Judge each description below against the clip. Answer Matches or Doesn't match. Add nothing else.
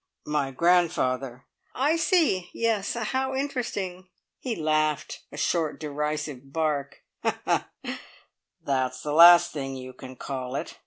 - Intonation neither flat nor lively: Doesn't match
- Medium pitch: Matches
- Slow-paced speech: Matches